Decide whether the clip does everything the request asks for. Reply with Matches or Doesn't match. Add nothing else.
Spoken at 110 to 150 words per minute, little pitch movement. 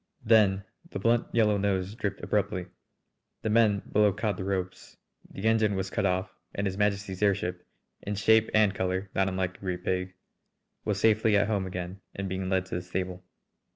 Doesn't match